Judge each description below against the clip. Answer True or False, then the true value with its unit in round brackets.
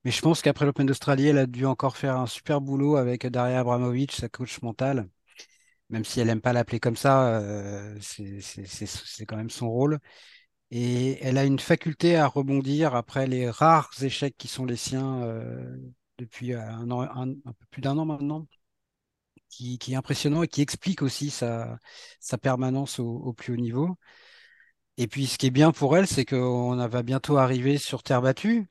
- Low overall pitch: True (130 Hz)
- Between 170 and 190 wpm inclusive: False (200 wpm)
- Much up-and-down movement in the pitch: False (2.9 semitones)